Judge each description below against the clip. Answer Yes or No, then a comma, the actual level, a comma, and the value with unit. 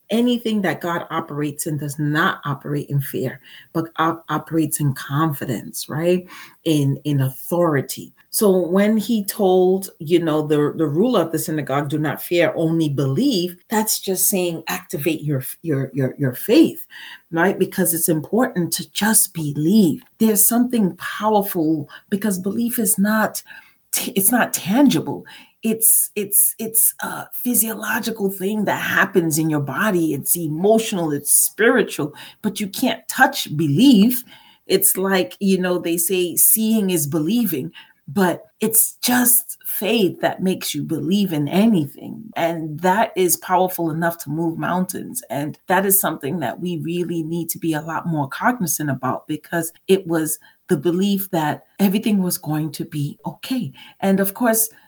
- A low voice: No, medium, 175 Hz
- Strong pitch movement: No, average, 4.8 semitones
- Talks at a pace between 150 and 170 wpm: Yes, average, 155 wpm